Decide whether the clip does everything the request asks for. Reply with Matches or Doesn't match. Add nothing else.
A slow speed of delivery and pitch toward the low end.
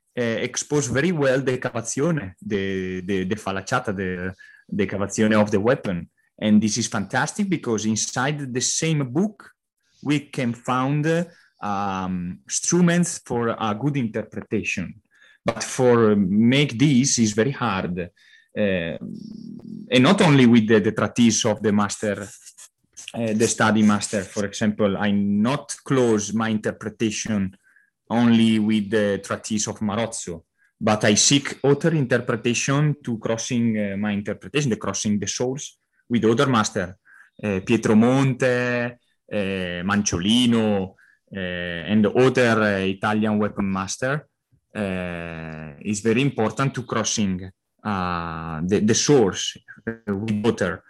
Matches